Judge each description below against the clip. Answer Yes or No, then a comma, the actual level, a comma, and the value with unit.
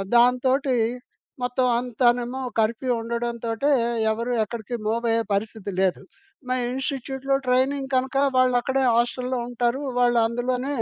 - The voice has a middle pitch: No, high, 245 Hz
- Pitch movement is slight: Yes, narrow, 1.9 semitones